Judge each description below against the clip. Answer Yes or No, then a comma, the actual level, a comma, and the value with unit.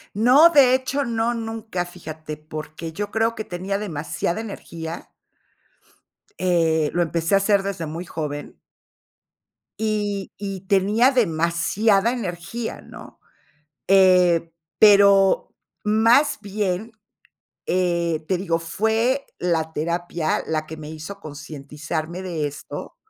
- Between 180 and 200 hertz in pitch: Yes, medium, 185 Hz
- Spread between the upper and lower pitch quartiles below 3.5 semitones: No, average, 4.8 semitones